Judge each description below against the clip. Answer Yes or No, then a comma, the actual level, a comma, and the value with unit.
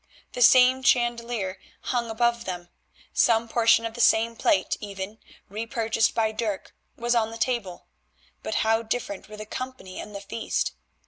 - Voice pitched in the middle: No, high, 225 Hz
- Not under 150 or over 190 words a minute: Yes, average, 155 wpm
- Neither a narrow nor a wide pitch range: No, narrow, 2.0 semitones